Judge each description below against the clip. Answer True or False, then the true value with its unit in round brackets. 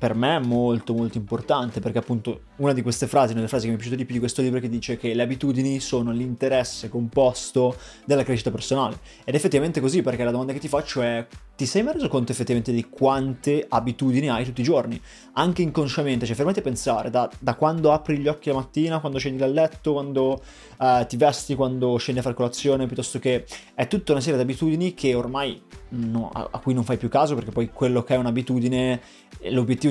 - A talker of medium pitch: False (130 Hz)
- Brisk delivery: True (225 wpm)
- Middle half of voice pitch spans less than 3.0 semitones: True (2.6 semitones)